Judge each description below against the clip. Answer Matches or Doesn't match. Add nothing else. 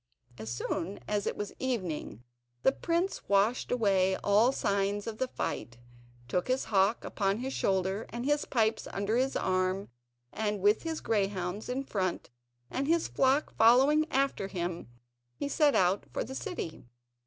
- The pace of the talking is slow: Doesn't match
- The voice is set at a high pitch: Matches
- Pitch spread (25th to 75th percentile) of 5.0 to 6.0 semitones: Matches